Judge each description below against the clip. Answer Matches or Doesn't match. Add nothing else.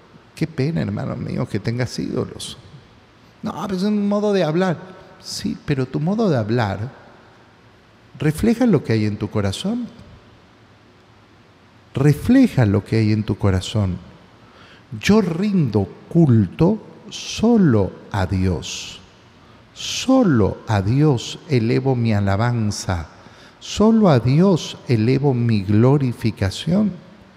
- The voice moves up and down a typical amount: Doesn't match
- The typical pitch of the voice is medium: Doesn't match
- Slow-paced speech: Matches